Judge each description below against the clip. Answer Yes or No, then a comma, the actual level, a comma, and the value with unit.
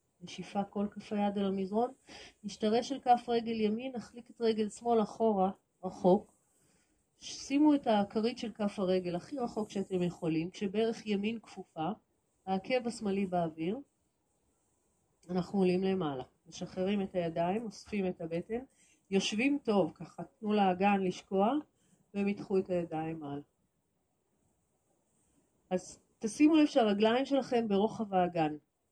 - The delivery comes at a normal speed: Yes, average, 120 wpm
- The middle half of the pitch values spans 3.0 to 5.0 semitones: Yes, average, 3.8 semitones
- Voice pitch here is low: No, high, 200 Hz